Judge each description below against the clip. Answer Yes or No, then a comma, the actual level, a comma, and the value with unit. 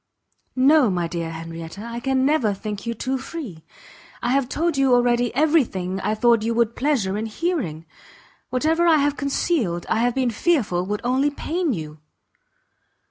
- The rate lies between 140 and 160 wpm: No, average, 175 wpm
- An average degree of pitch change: No, wide, 6.1 semitones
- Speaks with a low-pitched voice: No, high, 240 Hz